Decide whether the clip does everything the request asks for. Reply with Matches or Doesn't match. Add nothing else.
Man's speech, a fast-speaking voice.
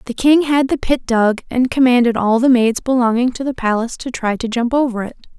Doesn't match